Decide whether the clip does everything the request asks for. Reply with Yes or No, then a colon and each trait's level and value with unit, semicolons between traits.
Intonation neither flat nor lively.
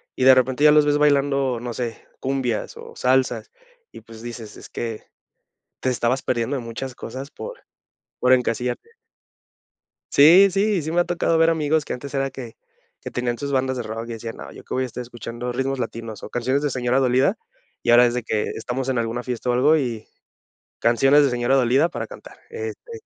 Yes: average, 3.1 semitones